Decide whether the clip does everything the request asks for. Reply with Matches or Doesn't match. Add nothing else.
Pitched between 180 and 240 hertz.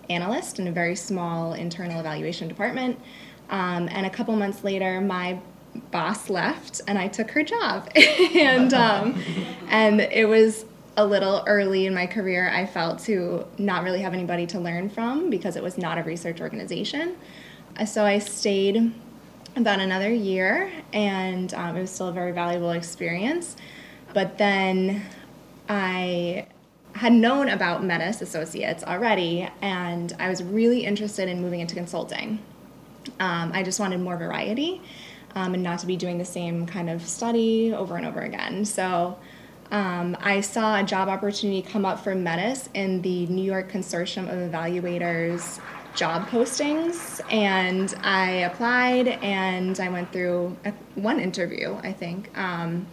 Matches